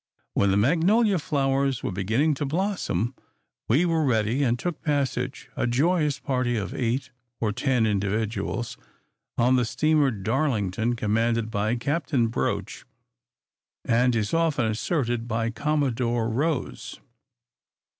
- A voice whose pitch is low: Yes, low, 125 Hz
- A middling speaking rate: No, slow, 125 wpm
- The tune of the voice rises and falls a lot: No, average, 4.6 semitones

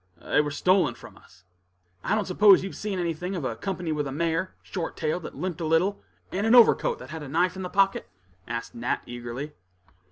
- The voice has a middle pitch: Yes, medium, 175 Hz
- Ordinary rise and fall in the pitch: Yes, average, 4.4 semitones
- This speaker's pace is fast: Yes, fast, 220 wpm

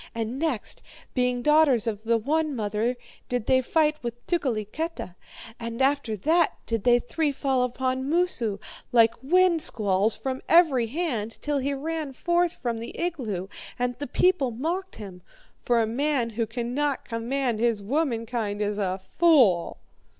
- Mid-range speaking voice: No, very high, 250 Hz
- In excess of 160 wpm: No, average, 150 wpm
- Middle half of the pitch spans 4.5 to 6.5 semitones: Yes, average, 5.0 semitones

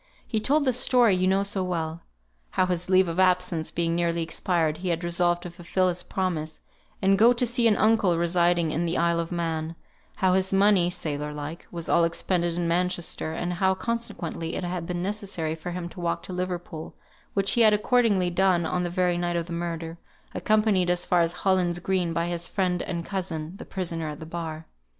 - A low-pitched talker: No, medium, 175 Hz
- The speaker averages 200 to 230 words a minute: Yes, fast, 205 wpm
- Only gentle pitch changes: Yes, narrow, 2.1 semitones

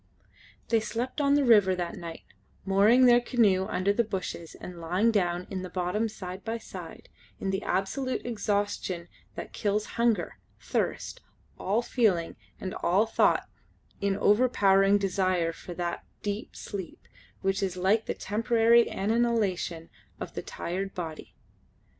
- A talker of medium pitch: No, high, 200 Hz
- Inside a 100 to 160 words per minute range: Yes, average, 145 wpm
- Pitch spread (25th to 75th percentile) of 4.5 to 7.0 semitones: No, average, 3.7 semitones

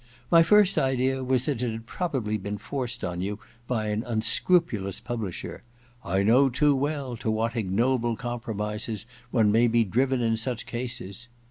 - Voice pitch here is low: Yes, low, 120 Hz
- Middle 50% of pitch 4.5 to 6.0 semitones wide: No, average, 3.3 semitones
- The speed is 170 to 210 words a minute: Yes, average, 175 wpm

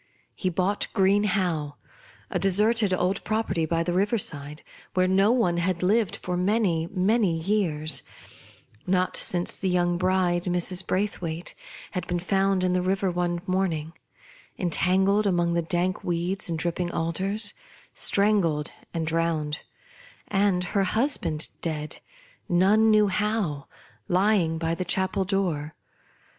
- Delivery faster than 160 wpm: No, slow, 135 wpm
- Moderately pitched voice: Yes, medium, 180 Hz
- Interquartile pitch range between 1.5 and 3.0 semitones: Yes, average, 2.7 semitones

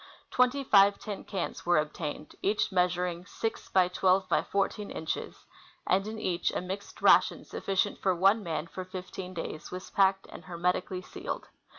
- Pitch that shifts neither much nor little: No, narrow, 2.0 semitones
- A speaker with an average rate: Yes, average, 165 wpm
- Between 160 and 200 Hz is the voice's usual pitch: Yes, medium, 185 Hz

